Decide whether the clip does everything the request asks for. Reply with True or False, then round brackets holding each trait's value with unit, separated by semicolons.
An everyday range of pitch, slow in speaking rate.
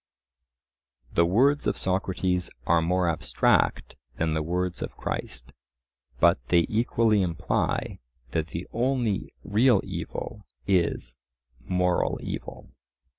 True (4.1 semitones; 110 wpm)